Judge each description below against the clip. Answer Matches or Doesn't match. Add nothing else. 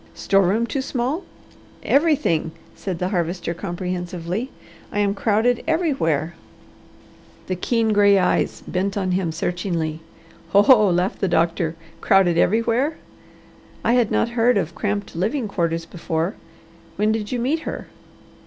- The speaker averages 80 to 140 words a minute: Matches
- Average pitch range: Matches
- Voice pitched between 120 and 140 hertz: Doesn't match